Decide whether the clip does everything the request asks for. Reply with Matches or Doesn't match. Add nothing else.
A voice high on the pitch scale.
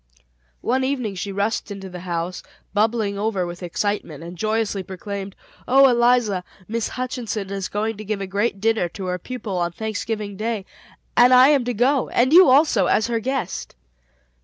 Matches